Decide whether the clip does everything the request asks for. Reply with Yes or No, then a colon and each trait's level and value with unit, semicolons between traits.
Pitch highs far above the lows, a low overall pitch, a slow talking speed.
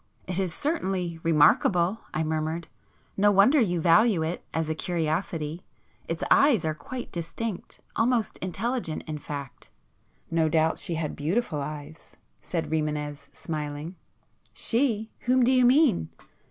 No: wide, 5.9 semitones; medium, 170 Hz; slow, 120 wpm